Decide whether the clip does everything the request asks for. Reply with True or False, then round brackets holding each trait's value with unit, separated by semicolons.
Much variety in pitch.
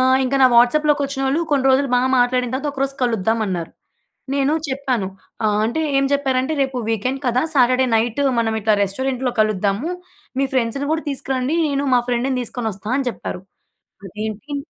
False (3.5 semitones)